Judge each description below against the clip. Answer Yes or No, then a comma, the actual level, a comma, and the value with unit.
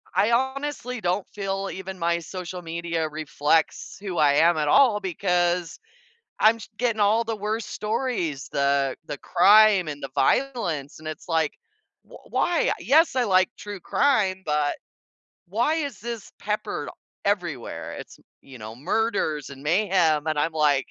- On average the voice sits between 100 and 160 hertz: No, medium, 185 Hz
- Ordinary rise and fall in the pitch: No, wide, 5.9 semitones